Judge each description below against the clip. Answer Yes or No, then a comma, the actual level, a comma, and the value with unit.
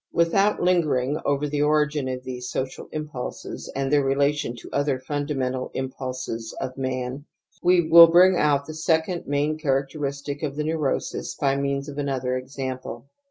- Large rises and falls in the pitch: No, narrow, 2.6 semitones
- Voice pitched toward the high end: No, medium, 140 Hz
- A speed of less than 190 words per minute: Yes, average, 165 wpm